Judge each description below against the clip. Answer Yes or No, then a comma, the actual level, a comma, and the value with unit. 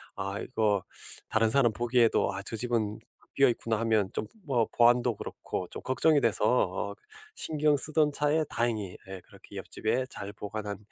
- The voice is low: Yes, low, 115 Hz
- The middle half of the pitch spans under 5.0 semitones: Yes, average, 3.8 semitones